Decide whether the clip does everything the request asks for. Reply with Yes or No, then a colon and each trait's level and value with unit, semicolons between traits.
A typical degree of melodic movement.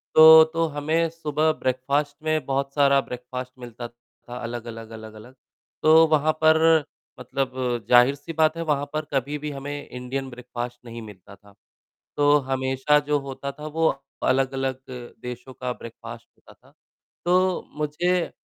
Yes: average, 3.7 semitones